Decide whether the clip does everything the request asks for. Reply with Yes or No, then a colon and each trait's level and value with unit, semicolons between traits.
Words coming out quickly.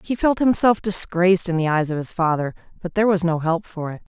Yes: fast, 245 wpm